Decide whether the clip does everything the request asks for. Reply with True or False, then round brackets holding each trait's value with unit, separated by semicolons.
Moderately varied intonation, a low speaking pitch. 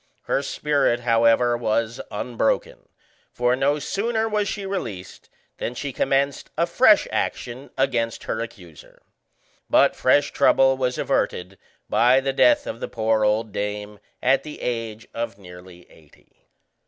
True (4.1 semitones; 120 Hz)